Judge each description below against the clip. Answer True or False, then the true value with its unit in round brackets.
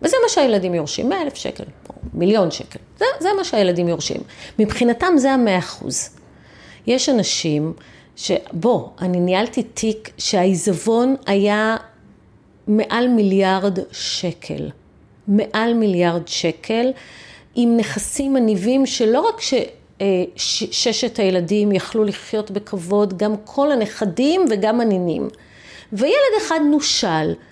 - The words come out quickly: False (115 wpm)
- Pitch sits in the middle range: False (215 Hz)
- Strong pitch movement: False (4.6 semitones)